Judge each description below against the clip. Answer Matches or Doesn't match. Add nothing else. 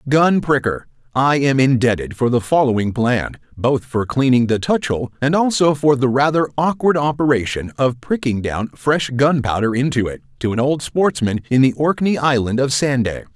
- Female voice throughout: Doesn't match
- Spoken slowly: Doesn't match